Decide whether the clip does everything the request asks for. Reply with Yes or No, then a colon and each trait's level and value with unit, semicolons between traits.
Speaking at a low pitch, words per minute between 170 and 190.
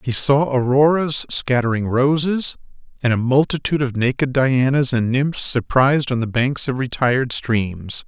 No: low, 130 Hz; average, 150 wpm